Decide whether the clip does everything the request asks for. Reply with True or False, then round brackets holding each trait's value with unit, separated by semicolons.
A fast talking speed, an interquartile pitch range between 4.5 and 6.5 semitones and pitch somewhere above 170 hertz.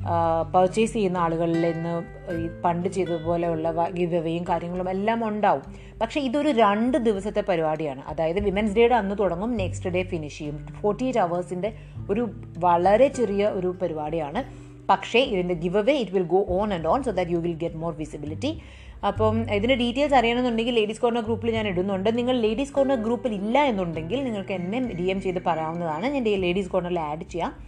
True (165 wpm; 5.0 semitones; 185 Hz)